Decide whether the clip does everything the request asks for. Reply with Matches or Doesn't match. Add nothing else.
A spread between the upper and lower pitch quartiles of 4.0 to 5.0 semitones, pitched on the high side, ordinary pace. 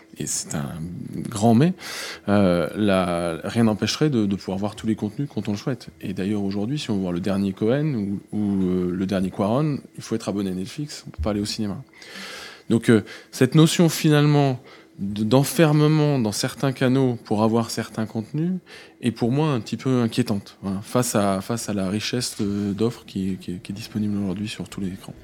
Doesn't match